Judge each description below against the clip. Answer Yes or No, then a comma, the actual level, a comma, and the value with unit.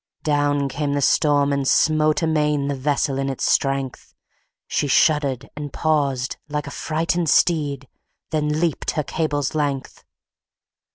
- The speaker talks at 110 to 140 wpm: Yes, slow, 135 wpm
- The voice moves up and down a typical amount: No, narrow, 1.8 semitones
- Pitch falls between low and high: Yes, medium, 145 Hz